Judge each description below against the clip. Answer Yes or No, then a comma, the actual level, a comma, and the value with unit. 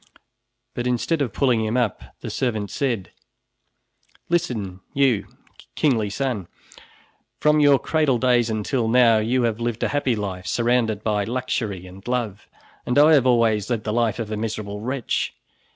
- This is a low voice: Yes, low, 120 Hz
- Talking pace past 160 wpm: No, average, 155 wpm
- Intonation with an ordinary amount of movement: Yes, average, 3.1 semitones